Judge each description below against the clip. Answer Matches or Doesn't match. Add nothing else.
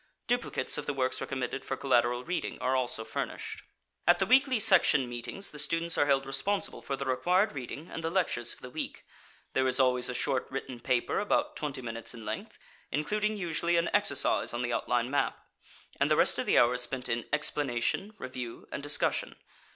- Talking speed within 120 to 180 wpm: Doesn't match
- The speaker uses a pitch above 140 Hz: Doesn't match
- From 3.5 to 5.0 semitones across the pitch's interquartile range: Doesn't match